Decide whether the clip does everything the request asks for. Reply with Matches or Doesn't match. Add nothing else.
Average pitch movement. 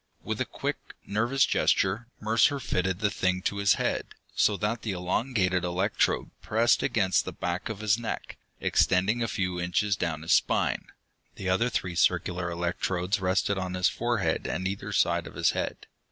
Matches